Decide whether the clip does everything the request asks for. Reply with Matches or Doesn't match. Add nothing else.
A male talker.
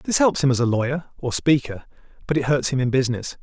Matches